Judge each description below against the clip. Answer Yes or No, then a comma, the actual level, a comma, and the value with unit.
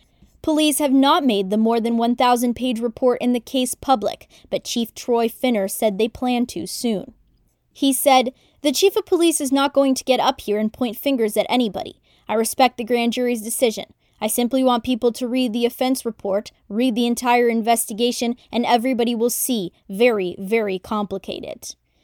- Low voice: No, high, 240 Hz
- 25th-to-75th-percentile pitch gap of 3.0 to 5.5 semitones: No, narrow, 2.4 semitones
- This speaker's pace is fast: No, average, 180 wpm